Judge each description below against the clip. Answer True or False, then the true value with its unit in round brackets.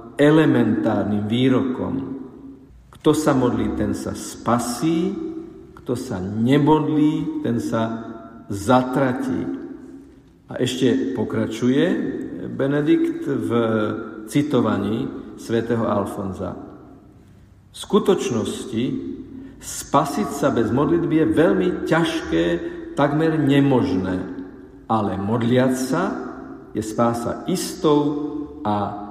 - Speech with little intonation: False (6.0 semitones)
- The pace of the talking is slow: True (80 wpm)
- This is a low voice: True (130 Hz)